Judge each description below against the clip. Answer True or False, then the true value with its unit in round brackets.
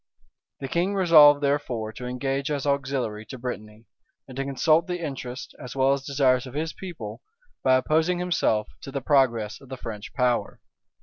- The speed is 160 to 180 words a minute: True (175 wpm)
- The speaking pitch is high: False (135 Hz)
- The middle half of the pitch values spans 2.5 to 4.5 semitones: True (3.0 semitones)